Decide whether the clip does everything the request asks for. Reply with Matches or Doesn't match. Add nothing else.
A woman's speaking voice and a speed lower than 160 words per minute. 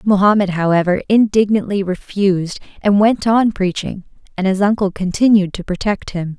Matches